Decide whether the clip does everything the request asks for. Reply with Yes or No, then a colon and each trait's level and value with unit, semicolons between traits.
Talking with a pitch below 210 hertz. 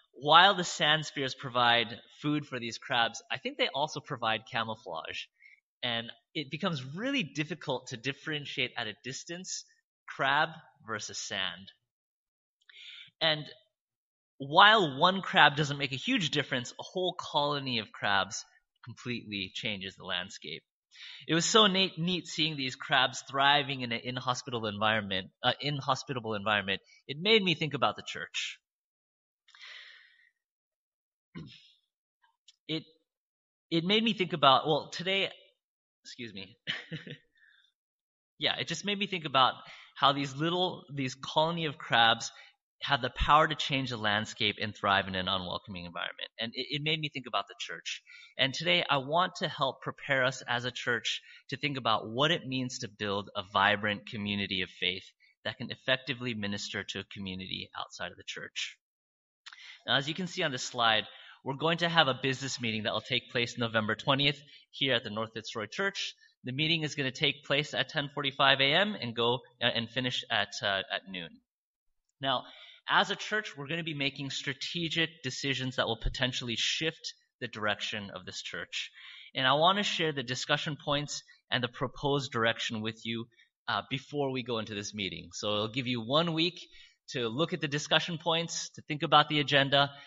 Yes: medium, 140 Hz